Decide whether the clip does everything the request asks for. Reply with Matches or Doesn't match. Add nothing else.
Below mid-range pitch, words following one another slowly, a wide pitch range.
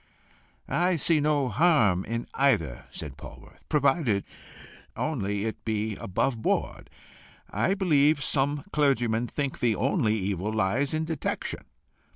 Matches